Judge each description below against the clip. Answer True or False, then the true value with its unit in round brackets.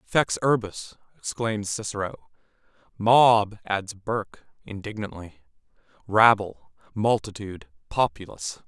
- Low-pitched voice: True (105 Hz)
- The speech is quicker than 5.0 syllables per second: False (4.2 syllables/s)